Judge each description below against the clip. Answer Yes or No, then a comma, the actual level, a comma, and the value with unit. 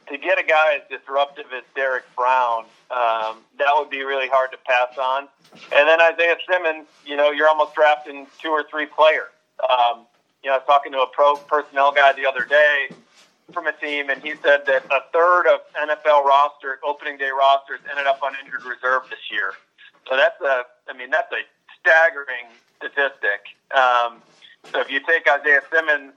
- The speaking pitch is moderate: Yes, medium, 145 Hz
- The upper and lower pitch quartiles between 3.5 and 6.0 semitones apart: No, narrow, 2.4 semitones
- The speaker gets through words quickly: No, average, 190 wpm